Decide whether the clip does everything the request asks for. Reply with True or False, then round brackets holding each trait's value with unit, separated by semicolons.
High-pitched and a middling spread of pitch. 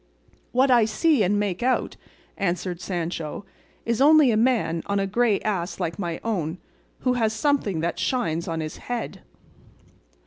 False (205 Hz; 5.9 semitones)